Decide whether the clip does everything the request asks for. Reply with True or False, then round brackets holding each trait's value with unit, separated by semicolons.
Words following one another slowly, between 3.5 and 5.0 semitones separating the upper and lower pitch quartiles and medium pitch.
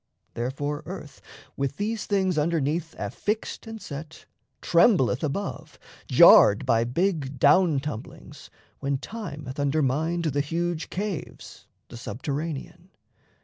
True (110 wpm; 4.2 semitones; 150 Hz)